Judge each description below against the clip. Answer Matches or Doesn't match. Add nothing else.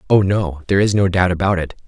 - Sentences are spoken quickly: Matches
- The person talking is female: Doesn't match